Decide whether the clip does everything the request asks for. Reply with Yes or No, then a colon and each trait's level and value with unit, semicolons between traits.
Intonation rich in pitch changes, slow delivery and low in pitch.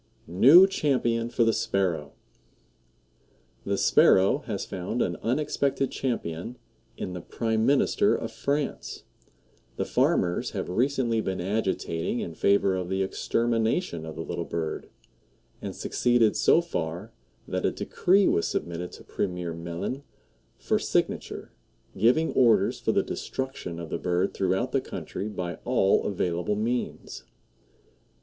Yes: wide, 5.8 semitones; slow, 130 wpm; low, 105 Hz